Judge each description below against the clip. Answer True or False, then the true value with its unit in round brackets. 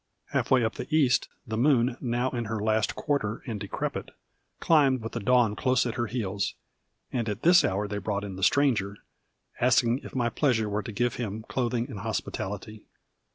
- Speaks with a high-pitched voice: False (115 Hz)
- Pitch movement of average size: True (3.3 semitones)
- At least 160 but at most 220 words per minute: True (190 wpm)